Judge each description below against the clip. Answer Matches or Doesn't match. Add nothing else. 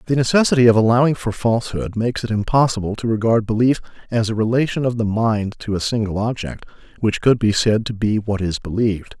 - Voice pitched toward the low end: Matches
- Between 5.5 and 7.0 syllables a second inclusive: Matches